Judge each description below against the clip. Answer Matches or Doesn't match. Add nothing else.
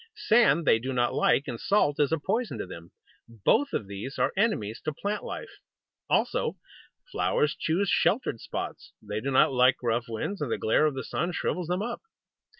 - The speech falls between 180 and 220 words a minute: Matches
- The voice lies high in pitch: Doesn't match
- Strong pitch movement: Matches